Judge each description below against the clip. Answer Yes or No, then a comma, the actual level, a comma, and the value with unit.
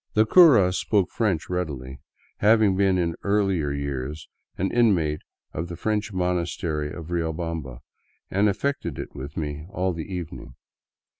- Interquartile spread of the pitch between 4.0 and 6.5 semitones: Yes, average, 4.7 semitones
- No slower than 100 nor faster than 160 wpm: Yes, average, 140 wpm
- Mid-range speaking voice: No, very low, 90 Hz